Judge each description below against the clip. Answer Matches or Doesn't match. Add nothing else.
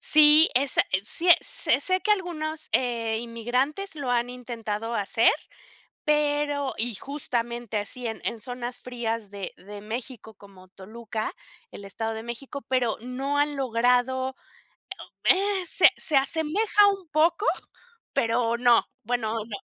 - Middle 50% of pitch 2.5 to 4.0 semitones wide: Doesn't match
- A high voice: Matches